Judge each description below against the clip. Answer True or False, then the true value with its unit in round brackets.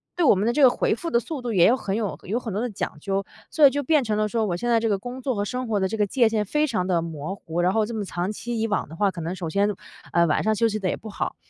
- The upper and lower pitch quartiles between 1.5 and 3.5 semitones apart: False (3.9 semitones)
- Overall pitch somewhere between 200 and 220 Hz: True (215 Hz)